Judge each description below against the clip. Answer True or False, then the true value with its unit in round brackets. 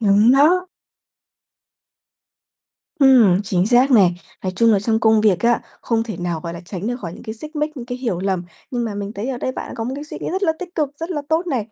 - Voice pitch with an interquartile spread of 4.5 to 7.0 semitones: True (5.4 semitones)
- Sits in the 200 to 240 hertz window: True (230 Hz)